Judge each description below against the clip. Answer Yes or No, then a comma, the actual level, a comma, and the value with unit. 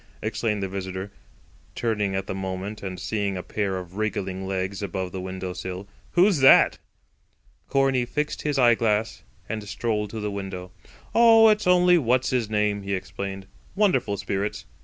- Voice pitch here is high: No, low, 100 Hz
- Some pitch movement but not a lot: Yes, average, 3.9 semitones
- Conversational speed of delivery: Yes, average, 160 wpm